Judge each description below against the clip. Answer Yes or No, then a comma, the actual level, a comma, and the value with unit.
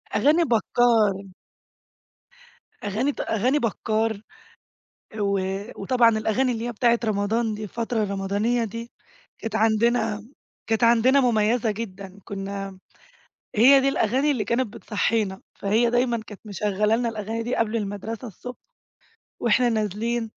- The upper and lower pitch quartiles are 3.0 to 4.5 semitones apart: No, narrow, 2.4 semitones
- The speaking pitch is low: No, high, 225 Hz